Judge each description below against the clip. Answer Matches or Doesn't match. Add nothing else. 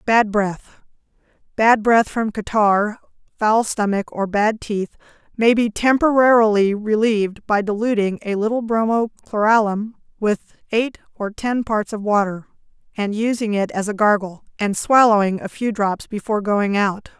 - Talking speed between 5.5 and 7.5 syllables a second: Doesn't match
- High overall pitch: Matches